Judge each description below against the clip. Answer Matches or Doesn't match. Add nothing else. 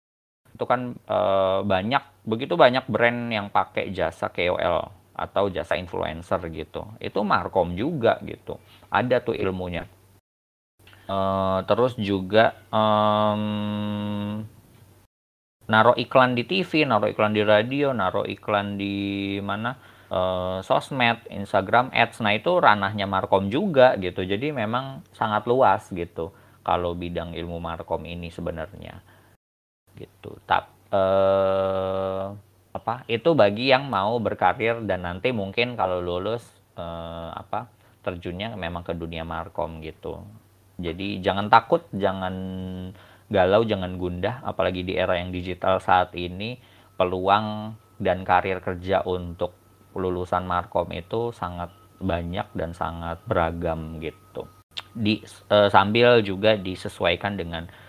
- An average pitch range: Matches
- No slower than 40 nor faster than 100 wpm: Doesn't match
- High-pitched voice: Doesn't match